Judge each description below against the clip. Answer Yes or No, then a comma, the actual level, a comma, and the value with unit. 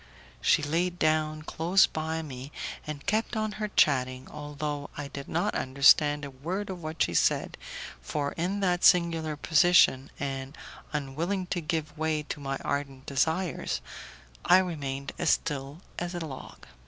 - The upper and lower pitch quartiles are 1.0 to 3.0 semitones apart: No, average, 3.7 semitones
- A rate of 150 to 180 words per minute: Yes, average, 155 wpm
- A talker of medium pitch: Yes, medium, 155 Hz